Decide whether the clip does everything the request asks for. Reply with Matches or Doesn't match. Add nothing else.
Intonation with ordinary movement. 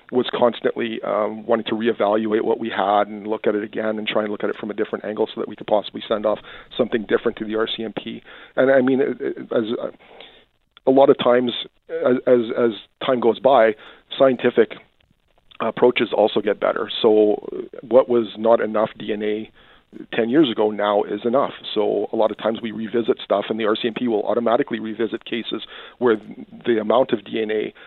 Doesn't match